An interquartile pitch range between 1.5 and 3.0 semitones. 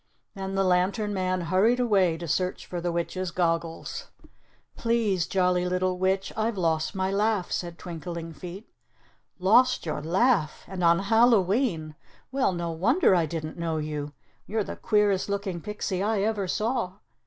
No: average, 3.4 semitones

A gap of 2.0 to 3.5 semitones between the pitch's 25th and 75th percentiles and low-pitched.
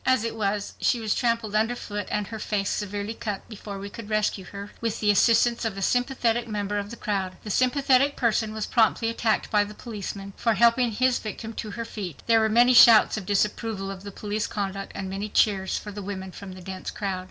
No: narrow, 2.5 semitones; high, 210 Hz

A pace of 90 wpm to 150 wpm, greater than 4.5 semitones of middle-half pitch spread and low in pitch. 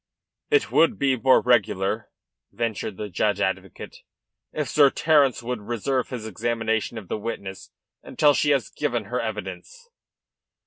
Yes: average, 140 wpm; average, 4.9 semitones; low, 120 Hz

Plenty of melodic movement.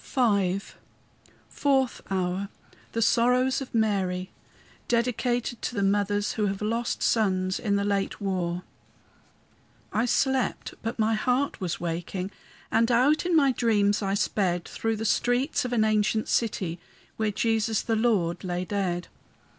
No: average, 3.6 semitones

